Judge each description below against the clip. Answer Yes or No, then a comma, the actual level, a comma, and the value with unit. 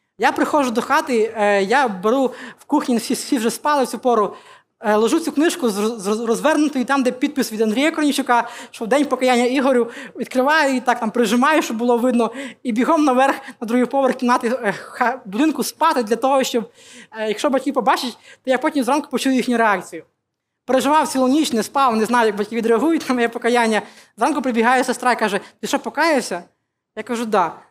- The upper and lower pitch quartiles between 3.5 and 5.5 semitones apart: No, average, 2.9 semitones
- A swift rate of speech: Yes, fast, 185 wpm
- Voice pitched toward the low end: No, very high, 250 Hz